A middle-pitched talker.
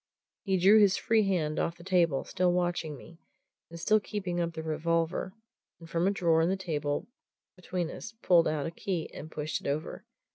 Yes: medium, 170 Hz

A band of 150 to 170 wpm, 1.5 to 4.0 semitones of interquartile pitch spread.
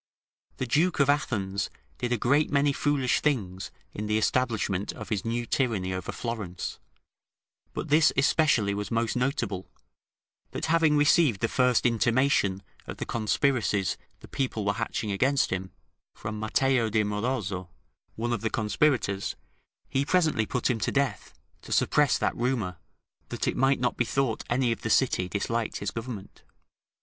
No: average, 160 wpm; average, 4.5 semitones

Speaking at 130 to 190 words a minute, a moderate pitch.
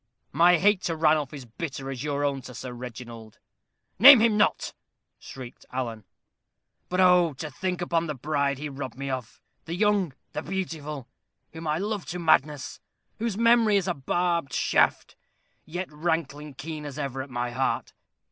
Yes: average, 165 wpm; medium, 150 Hz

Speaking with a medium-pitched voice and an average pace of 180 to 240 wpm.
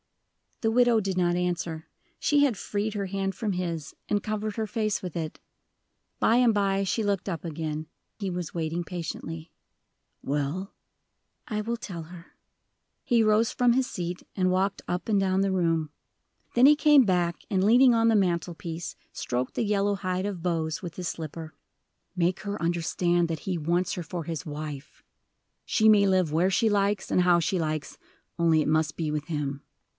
Yes: medium, 180 Hz; average, 185 wpm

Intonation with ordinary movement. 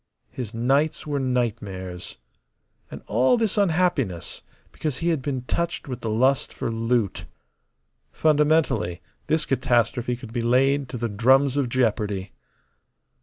Yes: average, 4.0 semitones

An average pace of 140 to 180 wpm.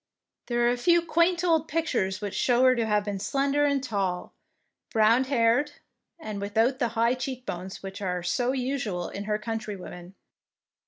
Yes: average, 170 wpm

